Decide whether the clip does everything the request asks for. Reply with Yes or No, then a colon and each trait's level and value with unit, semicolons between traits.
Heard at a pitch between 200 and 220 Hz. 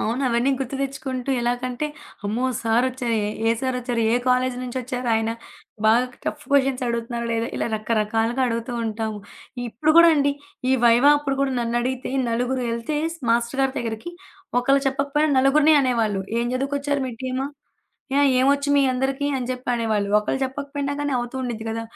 No: very high, 255 Hz